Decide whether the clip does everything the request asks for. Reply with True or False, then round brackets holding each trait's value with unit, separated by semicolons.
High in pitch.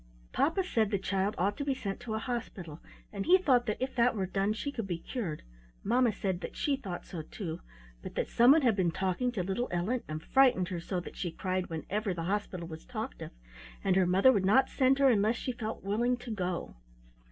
True (205 Hz)